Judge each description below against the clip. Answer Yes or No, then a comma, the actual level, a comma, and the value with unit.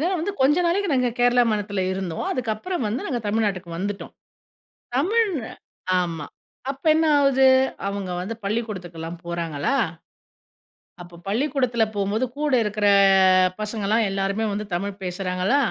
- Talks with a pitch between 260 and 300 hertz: No, high, 210 Hz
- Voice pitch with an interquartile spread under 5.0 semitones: No, wide, 5.5 semitones